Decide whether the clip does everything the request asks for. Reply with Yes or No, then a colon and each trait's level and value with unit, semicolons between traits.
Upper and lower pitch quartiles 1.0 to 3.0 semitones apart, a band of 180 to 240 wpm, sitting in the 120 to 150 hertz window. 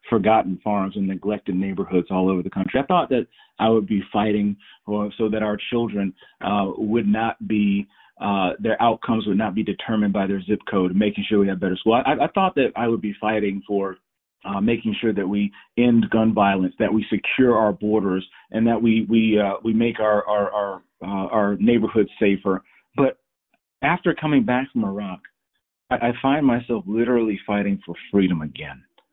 No: narrow, 2.4 semitones; average, 190 wpm; low, 105 Hz